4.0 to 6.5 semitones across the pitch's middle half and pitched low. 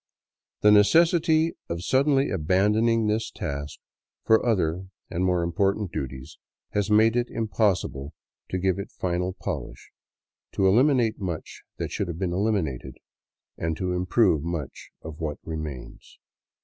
Yes: average, 5.0 semitones; very low, 95 Hz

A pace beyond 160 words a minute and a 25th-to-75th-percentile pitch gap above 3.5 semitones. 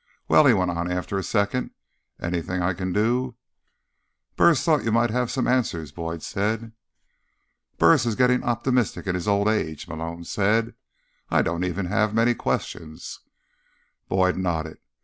No: average, 150 wpm; average, 5.2 semitones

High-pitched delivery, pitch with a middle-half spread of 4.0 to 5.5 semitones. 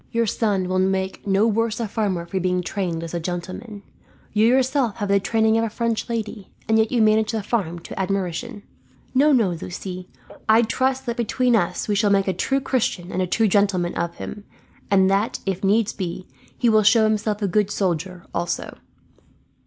No: high, 205 Hz; average, 3.4 semitones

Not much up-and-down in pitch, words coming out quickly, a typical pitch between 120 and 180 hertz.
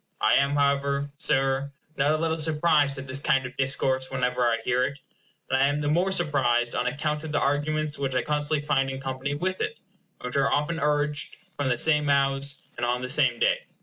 Yes: narrow, 2.1 semitones; fast, 215 wpm; medium, 140 Hz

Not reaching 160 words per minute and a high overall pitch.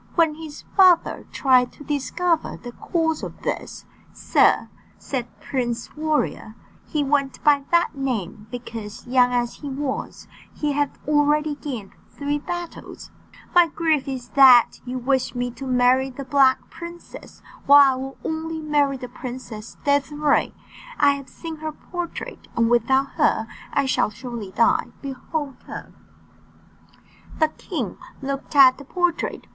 Yes: average, 140 wpm; very high, 275 Hz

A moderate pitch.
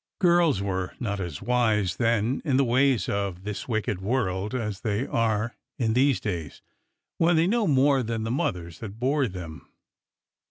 No: low, 115 Hz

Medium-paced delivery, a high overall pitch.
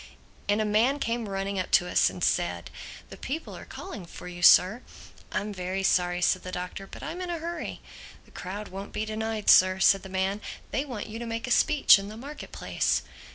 No: fast, 215 wpm; high, 205 Hz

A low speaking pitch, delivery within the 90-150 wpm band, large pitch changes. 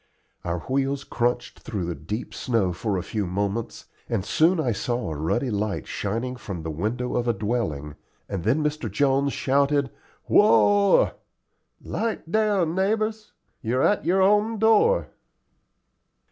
Yes: low, 125 Hz; average, 145 wpm; wide, 8.9 semitones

